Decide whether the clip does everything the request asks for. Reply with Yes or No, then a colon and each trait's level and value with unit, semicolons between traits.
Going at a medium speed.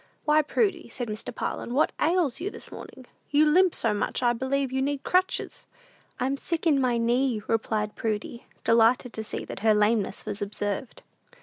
Yes: average, 185 wpm